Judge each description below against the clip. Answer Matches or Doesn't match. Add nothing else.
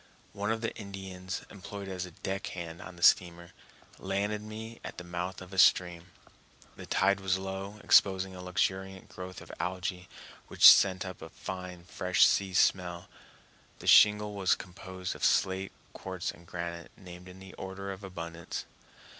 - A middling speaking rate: Matches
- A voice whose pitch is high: Doesn't match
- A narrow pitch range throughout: Matches